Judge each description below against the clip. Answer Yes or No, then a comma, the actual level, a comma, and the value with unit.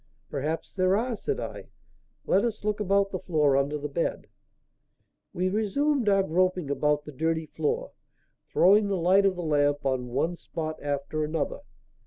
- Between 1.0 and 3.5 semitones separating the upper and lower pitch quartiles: No, average, 5.1 semitones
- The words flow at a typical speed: Yes, average, 165 wpm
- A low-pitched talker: No, medium, 175 Hz